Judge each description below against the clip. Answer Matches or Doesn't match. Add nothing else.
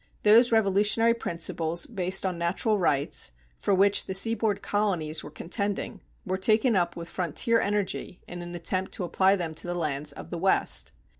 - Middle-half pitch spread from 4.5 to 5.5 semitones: Doesn't match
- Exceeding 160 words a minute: Matches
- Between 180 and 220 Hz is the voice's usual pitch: Matches